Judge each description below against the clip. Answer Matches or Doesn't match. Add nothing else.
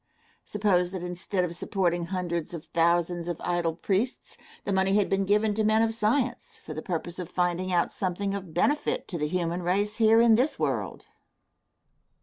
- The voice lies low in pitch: Doesn't match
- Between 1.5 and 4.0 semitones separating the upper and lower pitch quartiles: Matches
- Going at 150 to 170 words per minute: Doesn't match